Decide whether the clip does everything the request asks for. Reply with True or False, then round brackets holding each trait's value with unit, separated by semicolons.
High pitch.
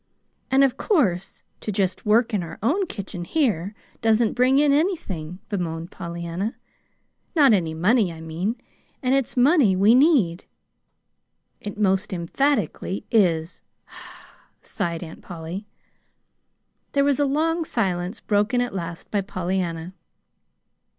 True (205 Hz)